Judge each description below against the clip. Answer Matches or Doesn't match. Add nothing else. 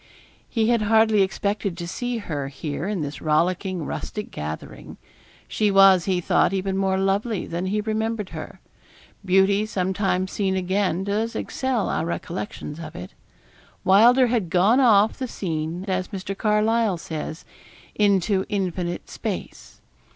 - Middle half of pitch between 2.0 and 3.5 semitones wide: Matches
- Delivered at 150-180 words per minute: Doesn't match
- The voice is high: Matches